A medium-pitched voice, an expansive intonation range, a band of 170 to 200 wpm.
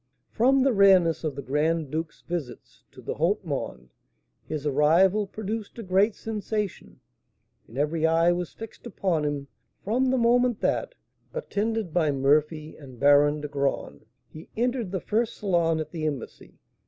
No: medium, 170 Hz; wide, 6.2 semitones; average, 155 wpm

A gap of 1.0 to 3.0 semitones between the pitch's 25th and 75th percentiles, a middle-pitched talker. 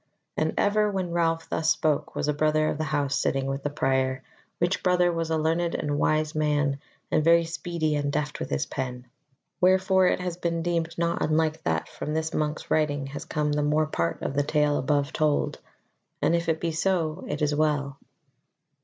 Yes: narrow, 2.4 semitones; medium, 155 Hz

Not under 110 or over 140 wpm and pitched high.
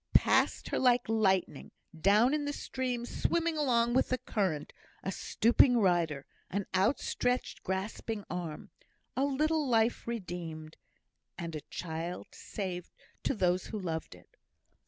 Yes: slow, 135 wpm; high, 210 Hz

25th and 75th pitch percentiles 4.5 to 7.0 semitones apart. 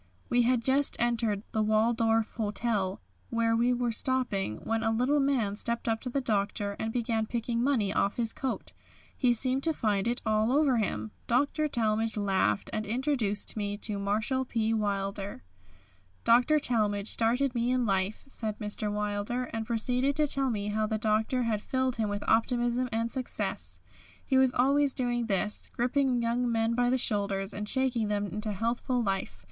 No: average, 3.0 semitones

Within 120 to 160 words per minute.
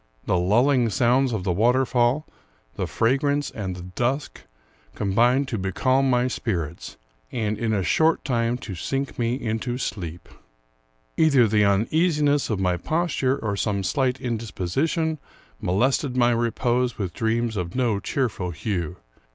Yes: average, 145 wpm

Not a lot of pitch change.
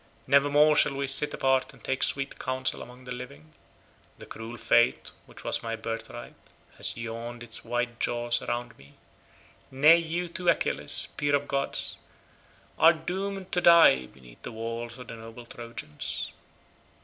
No: average, 3.8 semitones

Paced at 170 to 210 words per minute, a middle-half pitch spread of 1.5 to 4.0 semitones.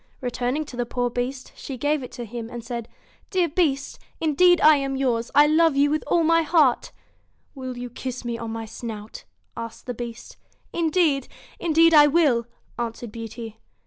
No: average, 180 wpm; average, 4.4 semitones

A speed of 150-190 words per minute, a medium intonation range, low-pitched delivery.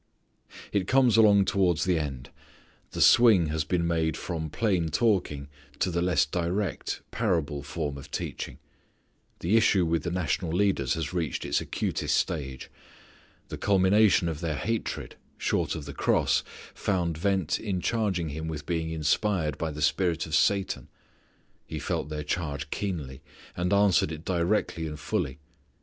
Yes: average, 155 wpm; average, 4.0 semitones; very low, 85 Hz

